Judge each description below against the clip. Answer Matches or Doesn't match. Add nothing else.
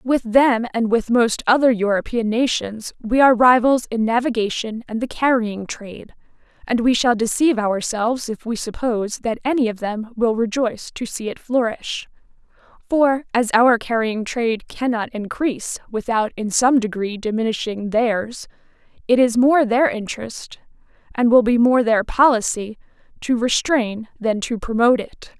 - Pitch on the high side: Matches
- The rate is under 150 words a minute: Doesn't match